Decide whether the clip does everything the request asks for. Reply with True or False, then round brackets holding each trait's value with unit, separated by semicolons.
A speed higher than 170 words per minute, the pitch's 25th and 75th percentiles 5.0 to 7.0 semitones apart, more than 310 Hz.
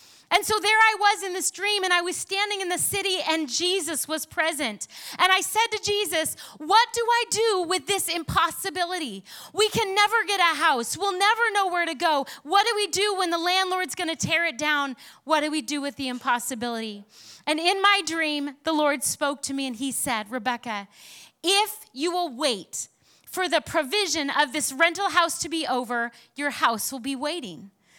True (200 wpm; 5.6 semitones; 335 Hz)